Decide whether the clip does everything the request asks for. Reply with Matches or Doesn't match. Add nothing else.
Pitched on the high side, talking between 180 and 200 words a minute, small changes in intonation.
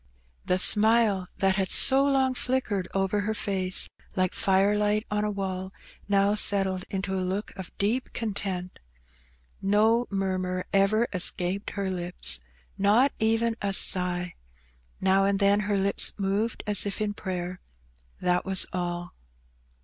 Doesn't match